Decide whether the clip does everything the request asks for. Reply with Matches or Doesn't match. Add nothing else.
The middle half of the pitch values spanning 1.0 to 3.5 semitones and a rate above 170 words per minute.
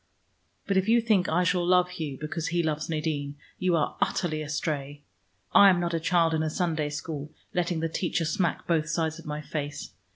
Matches